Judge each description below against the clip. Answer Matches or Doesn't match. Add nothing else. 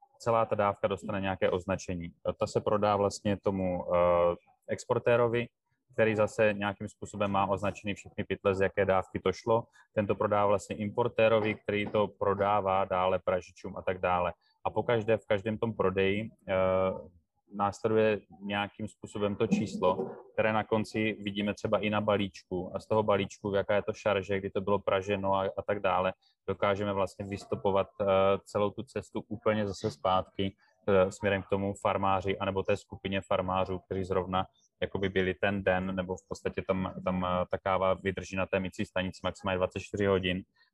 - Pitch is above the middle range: Doesn't match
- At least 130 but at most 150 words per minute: Doesn't match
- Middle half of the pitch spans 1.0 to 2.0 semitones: Matches